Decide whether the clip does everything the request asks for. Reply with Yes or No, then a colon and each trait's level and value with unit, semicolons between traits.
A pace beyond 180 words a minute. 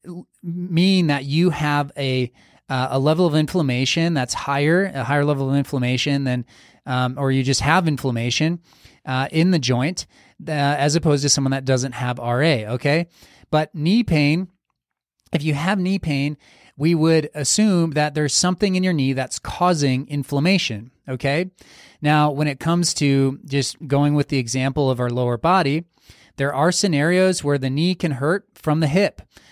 No: average, 170 wpm